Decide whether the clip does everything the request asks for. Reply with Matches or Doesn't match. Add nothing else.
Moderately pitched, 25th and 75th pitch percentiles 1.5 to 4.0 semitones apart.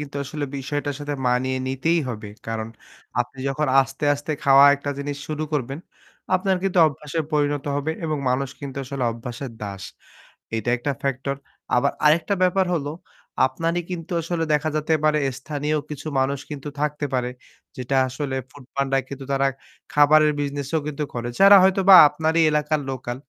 Matches